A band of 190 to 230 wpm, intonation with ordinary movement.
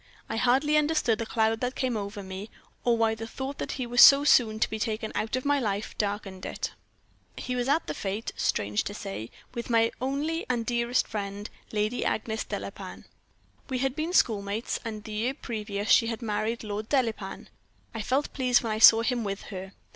Yes: average, 200 wpm; average, 3.1 semitones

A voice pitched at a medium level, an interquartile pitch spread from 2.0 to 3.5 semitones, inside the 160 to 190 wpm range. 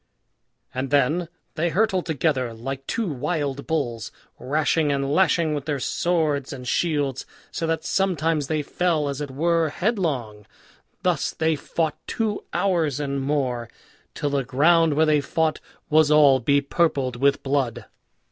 No: medium, 150 Hz; average, 3.1 semitones; average, 145 wpm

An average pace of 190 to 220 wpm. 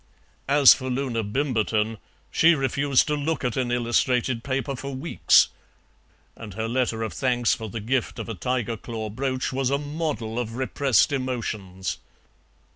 No: average, 155 wpm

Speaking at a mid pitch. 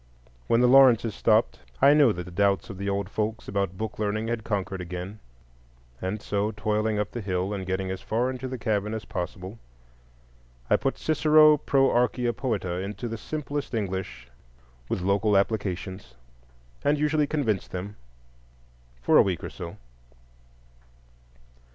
No: low, 105 Hz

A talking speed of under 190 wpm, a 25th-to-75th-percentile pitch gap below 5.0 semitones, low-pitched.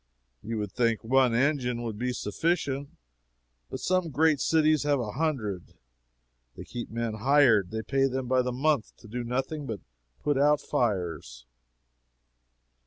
Yes: average, 150 wpm; average, 4.4 semitones; low, 125 Hz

